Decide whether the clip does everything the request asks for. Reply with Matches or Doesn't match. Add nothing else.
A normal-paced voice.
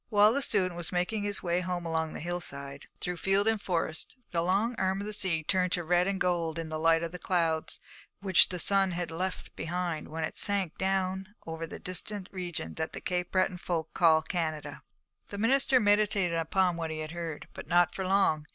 Doesn't match